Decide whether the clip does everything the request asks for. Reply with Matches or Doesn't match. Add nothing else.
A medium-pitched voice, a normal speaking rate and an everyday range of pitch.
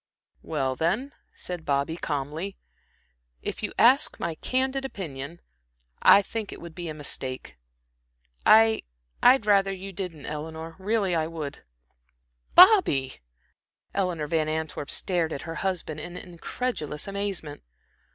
Doesn't match